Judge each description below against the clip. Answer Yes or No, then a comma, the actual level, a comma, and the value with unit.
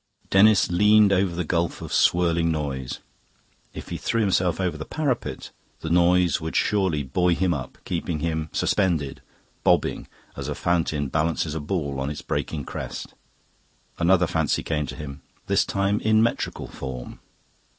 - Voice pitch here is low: Yes, very low, 85 Hz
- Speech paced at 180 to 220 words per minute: No, average, 155 wpm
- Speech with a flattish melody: No, average, 3.9 semitones